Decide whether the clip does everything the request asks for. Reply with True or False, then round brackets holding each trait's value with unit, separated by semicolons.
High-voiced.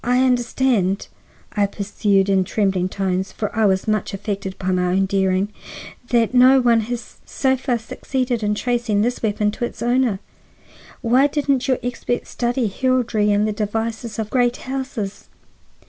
True (225 Hz)